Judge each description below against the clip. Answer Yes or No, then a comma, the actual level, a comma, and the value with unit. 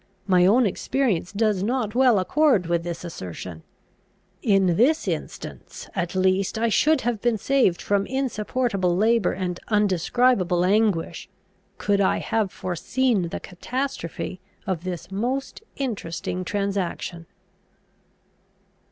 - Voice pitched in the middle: No, high, 200 Hz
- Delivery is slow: Yes, slow, 115 wpm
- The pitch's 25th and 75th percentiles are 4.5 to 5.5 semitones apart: Yes, average, 5.0 semitones